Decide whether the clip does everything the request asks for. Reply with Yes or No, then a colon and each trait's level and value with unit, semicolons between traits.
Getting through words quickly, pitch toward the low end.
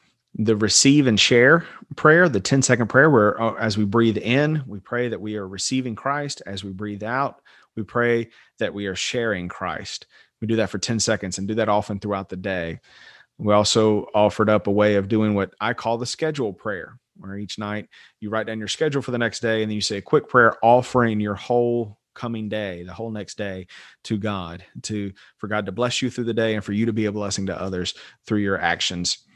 Yes: fast, 225 wpm; low, 110 Hz